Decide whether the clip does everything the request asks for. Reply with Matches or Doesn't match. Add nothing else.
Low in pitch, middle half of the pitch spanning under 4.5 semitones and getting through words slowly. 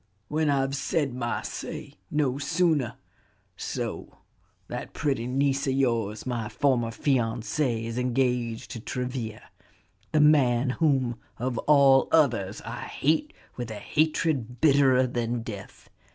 Matches